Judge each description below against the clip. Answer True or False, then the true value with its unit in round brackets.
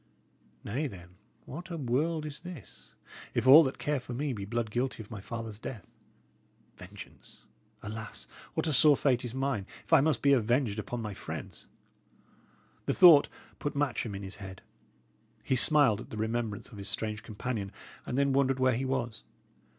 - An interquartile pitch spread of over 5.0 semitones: False (4.6 semitones)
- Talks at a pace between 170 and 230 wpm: True (175 wpm)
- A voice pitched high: False (125 Hz)